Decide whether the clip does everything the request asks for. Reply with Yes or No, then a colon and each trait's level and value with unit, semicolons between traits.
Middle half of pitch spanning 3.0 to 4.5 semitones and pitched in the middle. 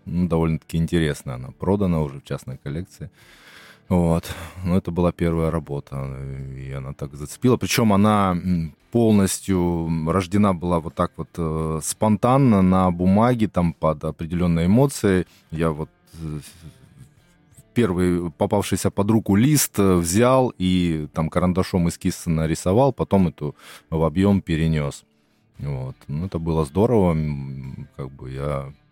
No: average, 4.0 semitones; very low, 85 Hz